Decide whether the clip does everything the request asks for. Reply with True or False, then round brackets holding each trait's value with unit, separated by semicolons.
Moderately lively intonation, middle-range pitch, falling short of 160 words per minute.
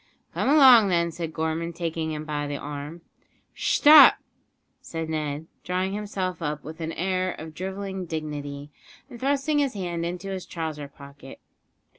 True (3.8 semitones; 170 Hz; 150 wpm)